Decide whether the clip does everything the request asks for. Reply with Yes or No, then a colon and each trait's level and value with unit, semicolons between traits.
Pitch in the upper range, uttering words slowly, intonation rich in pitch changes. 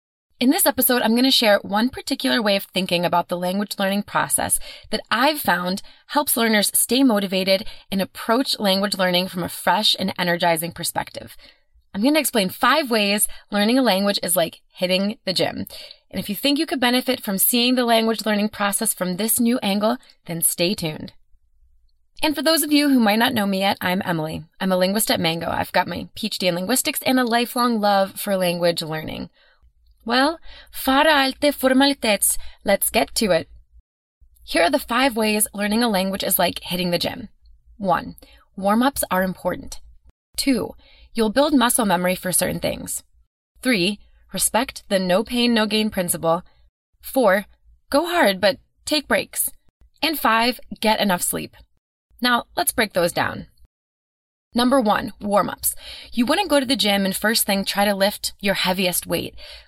No: high, 205 Hz; average, 175 wpm; wide, 5.7 semitones